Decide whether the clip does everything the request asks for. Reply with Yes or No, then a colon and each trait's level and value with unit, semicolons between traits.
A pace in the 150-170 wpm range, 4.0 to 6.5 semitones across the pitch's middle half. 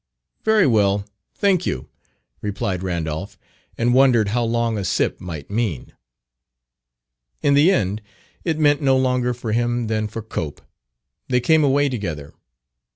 No: average, 140 wpm; average, 5.1 semitones